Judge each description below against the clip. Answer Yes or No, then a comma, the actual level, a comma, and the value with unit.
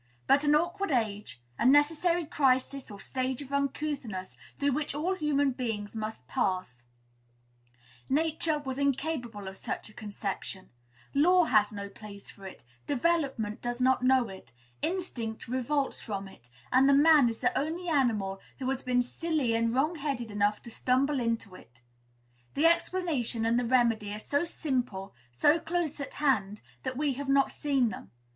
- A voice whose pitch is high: Yes, very high, 255 Hz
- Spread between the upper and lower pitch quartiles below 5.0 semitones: No, wide, 5.6 semitones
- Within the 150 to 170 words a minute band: Yes, average, 160 wpm